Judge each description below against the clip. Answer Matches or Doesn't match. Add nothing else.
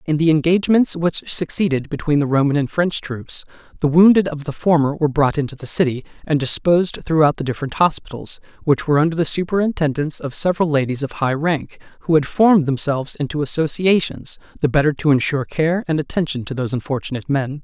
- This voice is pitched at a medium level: Matches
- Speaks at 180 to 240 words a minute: Matches